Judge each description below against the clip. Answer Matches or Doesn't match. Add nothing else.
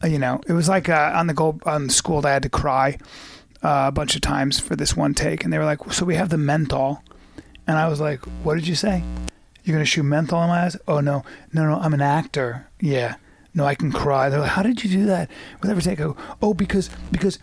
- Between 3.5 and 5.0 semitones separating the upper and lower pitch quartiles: Matches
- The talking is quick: Matches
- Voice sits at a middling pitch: Matches